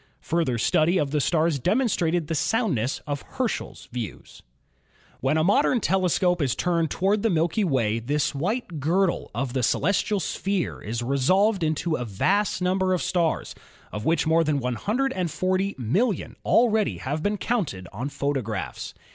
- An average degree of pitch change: No, wide, 5.9 semitones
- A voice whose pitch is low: No, medium, 165 Hz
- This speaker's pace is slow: No, average, 145 wpm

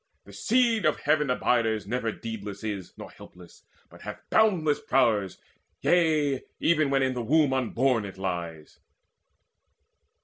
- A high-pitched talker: No, low, 125 Hz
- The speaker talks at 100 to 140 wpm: Yes, slow, 135 wpm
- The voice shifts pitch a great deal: Yes, wide, 6.5 semitones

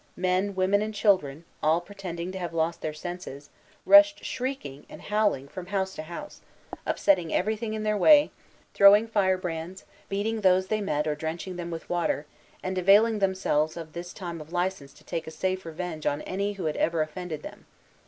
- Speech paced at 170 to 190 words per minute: Yes, average, 185 wpm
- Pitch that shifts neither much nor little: Yes, average, 3.6 semitones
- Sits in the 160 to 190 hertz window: Yes, medium, 185 Hz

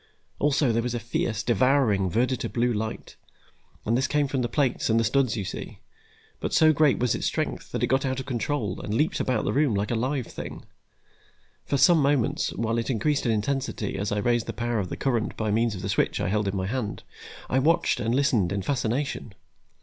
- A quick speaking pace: Yes, fast, 220 wpm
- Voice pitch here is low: Yes, low, 120 Hz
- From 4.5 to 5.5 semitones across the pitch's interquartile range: No, average, 3.9 semitones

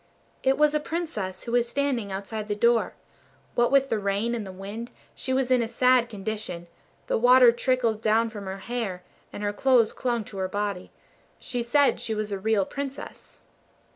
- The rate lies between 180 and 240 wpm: Yes, average, 190 wpm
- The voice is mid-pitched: No, high, 230 Hz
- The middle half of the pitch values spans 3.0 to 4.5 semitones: Yes, average, 3.7 semitones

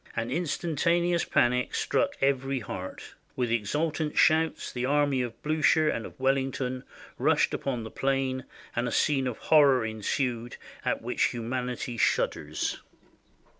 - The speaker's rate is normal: No, slow, 130 wpm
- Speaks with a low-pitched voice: Yes, low, 130 Hz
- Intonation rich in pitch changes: No, average, 3.3 semitones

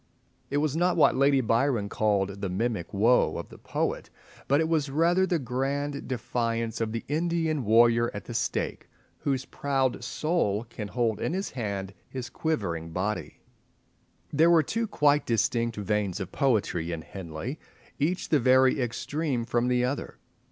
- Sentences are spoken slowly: No, average, 160 wpm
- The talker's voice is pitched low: Yes, low, 125 Hz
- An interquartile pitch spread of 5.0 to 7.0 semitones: Yes, average, 5.3 semitones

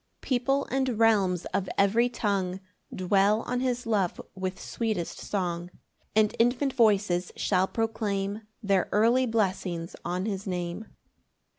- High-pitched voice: Yes, high, 205 Hz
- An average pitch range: Yes, average, 3.7 semitones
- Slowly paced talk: Yes, slow, 130 wpm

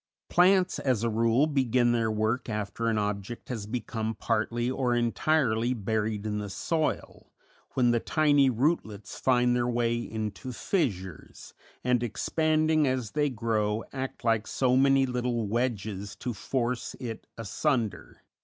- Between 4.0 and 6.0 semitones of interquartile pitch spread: No, average, 3.0 semitones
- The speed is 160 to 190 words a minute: No, average, 140 wpm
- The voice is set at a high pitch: No, low, 120 Hz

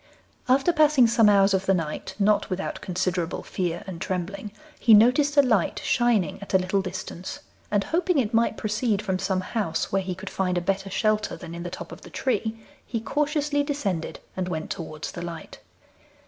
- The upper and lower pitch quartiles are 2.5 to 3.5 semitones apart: No, average, 4.2 semitones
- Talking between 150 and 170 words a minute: No, average, 190 wpm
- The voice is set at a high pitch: Yes, high, 195 Hz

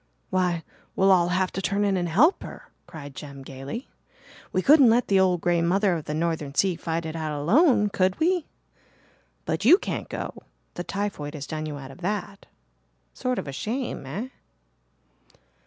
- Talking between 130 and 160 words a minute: No, average, 180 wpm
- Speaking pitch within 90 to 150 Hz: No, medium, 180 Hz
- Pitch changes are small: No, average, 4.7 semitones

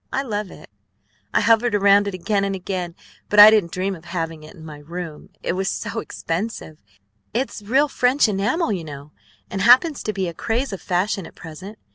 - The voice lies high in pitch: Yes, high, 195 Hz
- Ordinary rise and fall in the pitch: Yes, average, 4.3 semitones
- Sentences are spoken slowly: No, average, 200 wpm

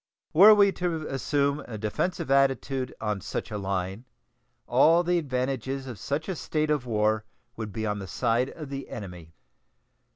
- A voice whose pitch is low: Yes, low, 130 Hz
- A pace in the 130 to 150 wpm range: No, average, 165 wpm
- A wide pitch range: Yes, wide, 5.9 semitones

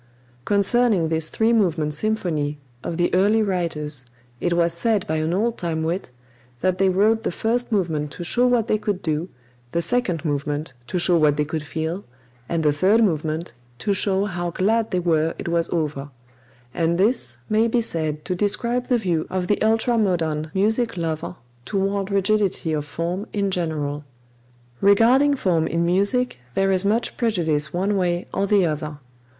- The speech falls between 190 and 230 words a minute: No, average, 175 wpm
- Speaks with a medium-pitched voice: Yes, medium, 180 Hz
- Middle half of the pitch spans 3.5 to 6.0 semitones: Yes, average, 4.7 semitones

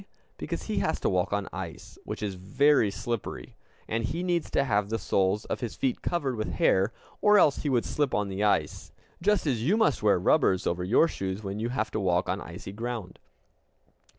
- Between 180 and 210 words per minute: Yes, fast, 205 wpm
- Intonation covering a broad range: Yes, wide, 6.0 semitones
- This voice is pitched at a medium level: No, low, 110 Hz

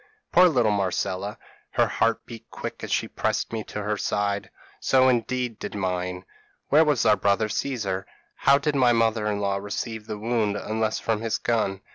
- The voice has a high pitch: No, low, 110 Hz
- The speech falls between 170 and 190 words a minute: Yes, average, 185 wpm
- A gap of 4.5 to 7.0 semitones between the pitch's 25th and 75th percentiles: No, average, 2.9 semitones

